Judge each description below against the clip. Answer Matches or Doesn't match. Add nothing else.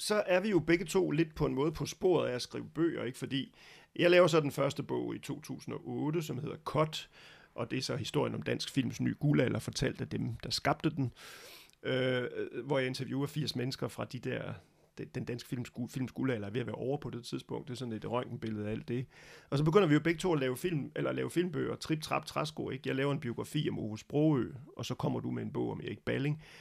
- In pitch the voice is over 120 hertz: Matches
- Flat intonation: Doesn't match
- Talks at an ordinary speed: Doesn't match